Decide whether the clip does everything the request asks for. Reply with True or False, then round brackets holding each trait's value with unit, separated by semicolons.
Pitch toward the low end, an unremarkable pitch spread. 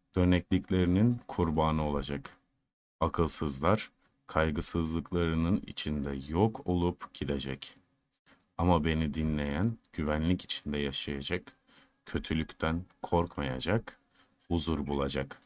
True (80 Hz; 3.6 semitones)